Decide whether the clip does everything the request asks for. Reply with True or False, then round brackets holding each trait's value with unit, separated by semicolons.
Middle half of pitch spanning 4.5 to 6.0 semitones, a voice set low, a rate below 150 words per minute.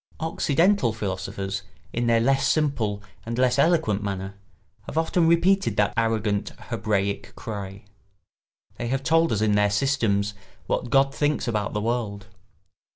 True (5.2 semitones; 115 Hz; 140 wpm)